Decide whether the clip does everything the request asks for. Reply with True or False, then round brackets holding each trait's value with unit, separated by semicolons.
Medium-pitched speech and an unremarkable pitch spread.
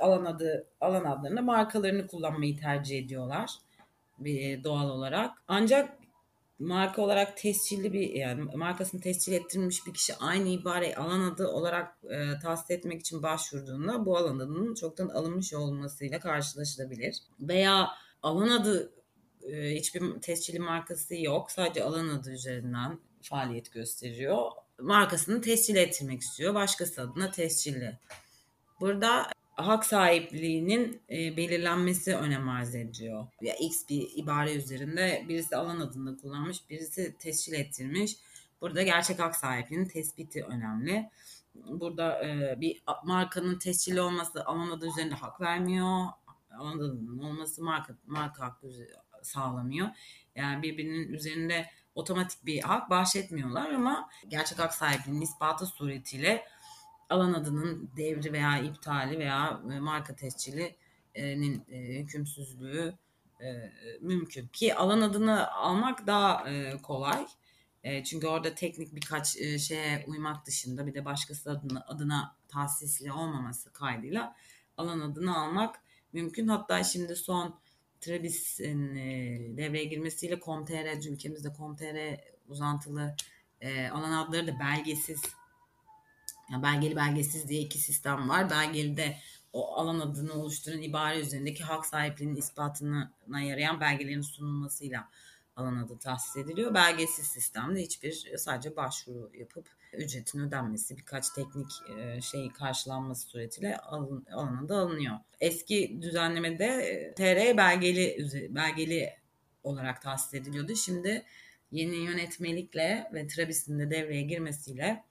True (155 Hz; 4.0 semitones)